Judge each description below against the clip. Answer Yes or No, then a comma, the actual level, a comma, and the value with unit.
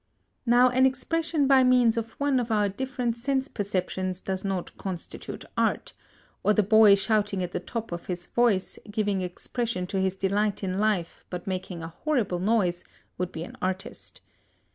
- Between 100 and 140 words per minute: No, average, 170 wpm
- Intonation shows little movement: No, average, 4.4 semitones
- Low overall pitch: No, high, 205 Hz